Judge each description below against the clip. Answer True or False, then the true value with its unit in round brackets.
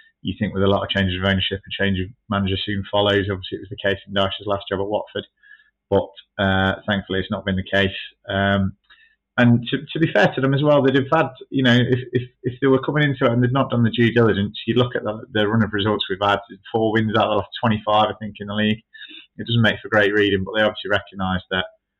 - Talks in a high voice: False (105 Hz)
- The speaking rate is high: True (260 wpm)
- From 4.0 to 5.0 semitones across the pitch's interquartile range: True (4.3 semitones)